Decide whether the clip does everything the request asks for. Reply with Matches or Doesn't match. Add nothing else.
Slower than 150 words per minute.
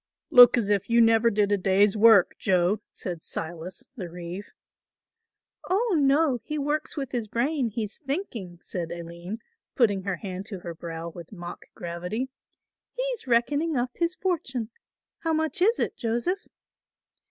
Doesn't match